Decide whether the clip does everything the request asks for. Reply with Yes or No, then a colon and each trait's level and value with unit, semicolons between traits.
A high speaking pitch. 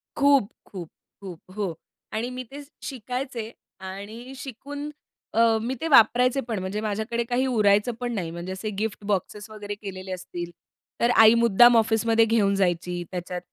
Yes: high, 220 Hz